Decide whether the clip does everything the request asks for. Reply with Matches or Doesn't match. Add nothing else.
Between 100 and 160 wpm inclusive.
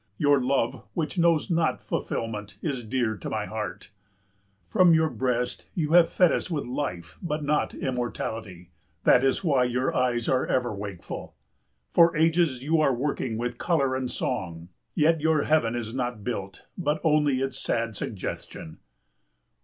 Matches